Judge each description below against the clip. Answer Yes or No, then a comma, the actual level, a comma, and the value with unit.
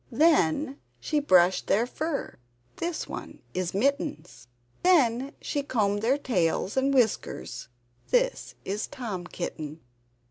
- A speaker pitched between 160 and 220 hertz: No, very high, 250 Hz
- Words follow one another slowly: Yes, slow, 115 wpm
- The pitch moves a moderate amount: No, wide, 7.3 semitones